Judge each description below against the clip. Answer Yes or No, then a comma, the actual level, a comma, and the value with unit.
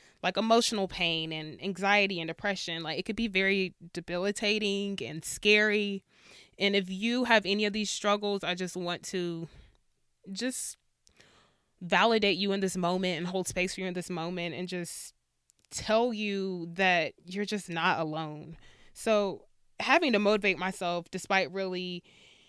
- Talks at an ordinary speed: Yes, average, 150 wpm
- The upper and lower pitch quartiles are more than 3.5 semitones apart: No, average, 2.8 semitones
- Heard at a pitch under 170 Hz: No, high, 190 Hz